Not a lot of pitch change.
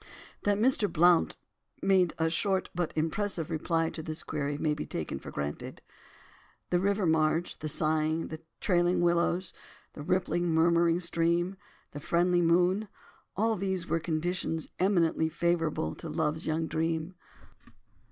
Yes: narrow, 2.0 semitones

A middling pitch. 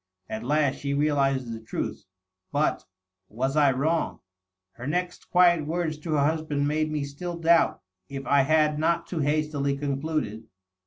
Yes: medium, 150 Hz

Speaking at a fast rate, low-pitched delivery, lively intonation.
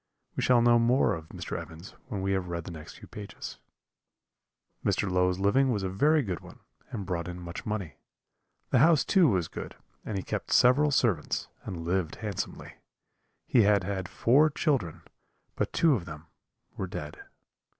No: average, 175 wpm; low, 100 Hz; wide, 5.7 semitones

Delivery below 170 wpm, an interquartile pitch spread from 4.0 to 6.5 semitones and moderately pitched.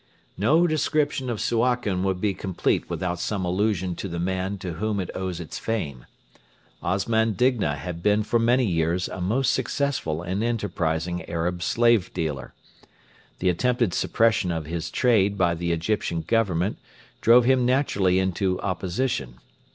No: average, 150 wpm; average, 4.7 semitones; very low, 95 Hz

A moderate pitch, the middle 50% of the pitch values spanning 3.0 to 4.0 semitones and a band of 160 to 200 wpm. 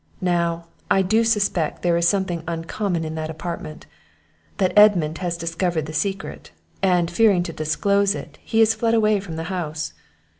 Yes: medium, 175 Hz; average, 3.5 semitones; average, 165 wpm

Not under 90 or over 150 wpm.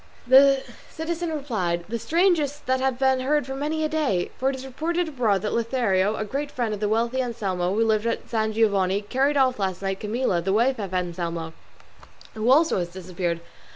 No: average, 195 wpm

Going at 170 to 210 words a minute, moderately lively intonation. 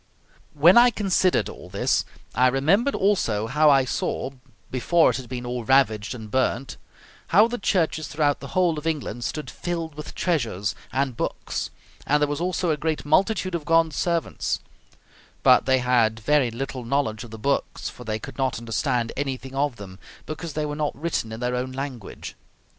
Yes: average, 180 wpm; average, 4.7 semitones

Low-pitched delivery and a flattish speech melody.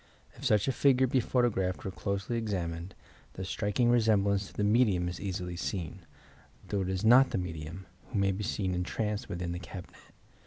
No: low, 100 Hz; average, 3.6 semitones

